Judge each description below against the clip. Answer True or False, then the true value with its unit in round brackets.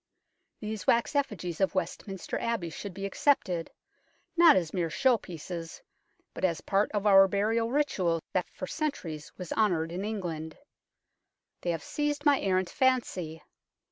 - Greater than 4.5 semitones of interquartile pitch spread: True (5.1 semitones)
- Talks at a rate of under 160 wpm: True (145 wpm)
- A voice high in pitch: True (195 Hz)